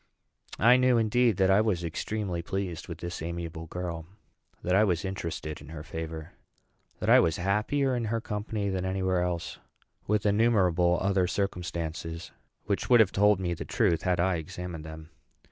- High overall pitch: No, very low, 90 Hz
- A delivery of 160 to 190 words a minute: Yes, average, 175 wpm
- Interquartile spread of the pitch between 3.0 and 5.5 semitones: Yes, average, 3.6 semitones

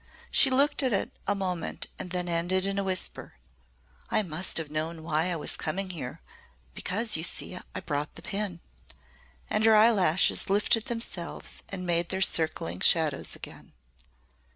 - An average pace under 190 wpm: Yes, average, 160 wpm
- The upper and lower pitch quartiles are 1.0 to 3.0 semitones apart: No, average, 3.6 semitones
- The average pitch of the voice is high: No, medium, 180 Hz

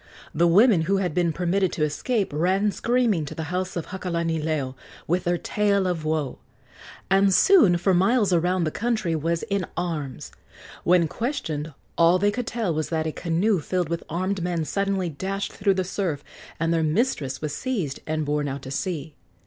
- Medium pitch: Yes, medium, 175 Hz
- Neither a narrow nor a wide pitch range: Yes, average, 3.8 semitones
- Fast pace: No, average, 180 wpm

